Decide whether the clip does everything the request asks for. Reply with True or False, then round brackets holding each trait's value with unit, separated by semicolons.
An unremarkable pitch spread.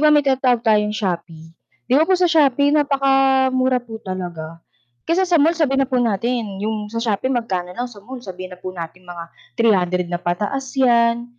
False (6.4 semitones)